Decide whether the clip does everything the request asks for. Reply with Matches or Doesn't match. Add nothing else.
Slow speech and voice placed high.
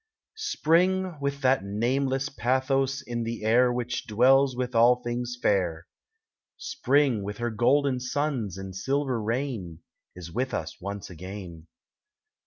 Doesn't match